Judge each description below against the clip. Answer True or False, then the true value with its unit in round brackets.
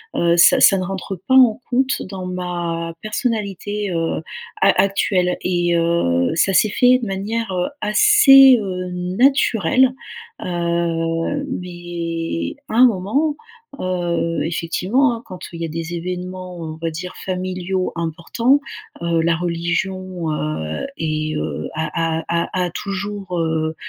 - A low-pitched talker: False (180 Hz)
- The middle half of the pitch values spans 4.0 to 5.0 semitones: False (3.2 semitones)